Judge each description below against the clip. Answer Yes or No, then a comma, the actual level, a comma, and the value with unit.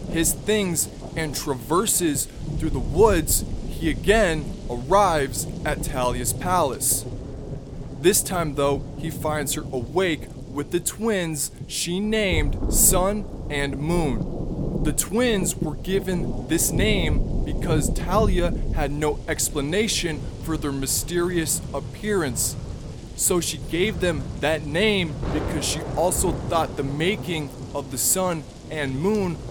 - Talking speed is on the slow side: Yes, slow, 120 wpm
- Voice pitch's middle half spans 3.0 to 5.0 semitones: Yes, average, 4.3 semitones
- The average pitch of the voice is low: No, medium, 150 Hz